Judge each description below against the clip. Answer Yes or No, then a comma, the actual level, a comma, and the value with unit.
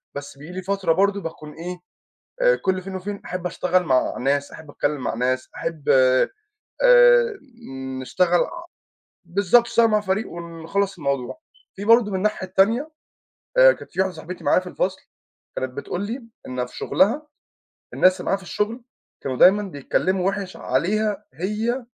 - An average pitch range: Yes, average, 4.4 semitones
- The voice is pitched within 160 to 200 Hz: Yes, medium, 185 Hz